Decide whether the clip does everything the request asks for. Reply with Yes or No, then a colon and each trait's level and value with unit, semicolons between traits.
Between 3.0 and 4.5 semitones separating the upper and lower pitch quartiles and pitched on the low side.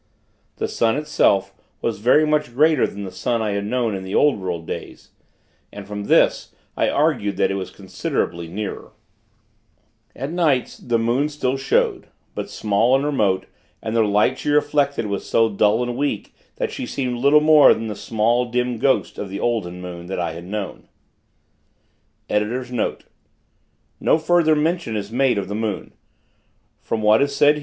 No: average, 5.2 semitones; low, 115 Hz